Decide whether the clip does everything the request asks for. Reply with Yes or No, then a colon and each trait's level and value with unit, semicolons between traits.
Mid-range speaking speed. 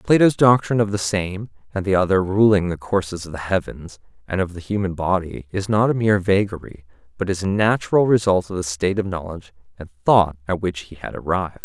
No: fast, 210 wpm